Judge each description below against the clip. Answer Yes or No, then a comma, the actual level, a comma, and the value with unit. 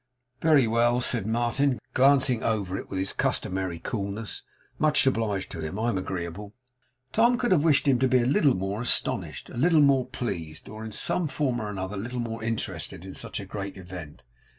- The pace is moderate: Yes, average, 195 wpm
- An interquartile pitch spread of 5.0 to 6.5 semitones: Yes, average, 5.3 semitones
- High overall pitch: No, low, 115 Hz